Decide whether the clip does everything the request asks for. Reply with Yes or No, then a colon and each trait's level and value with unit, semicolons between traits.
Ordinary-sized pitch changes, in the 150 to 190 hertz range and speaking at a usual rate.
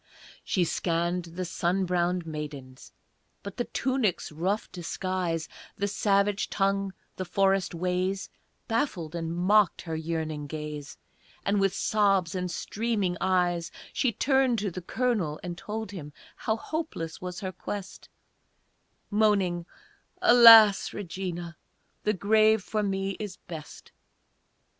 No: average, 3.3 semitones; medium, 185 Hz; slow, 125 wpm